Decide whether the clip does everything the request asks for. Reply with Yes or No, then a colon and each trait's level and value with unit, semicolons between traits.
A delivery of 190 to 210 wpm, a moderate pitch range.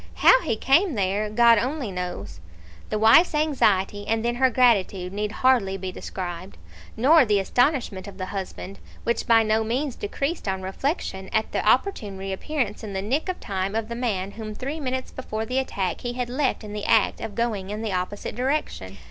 Yes: average, 195 wpm; average, 4.6 semitones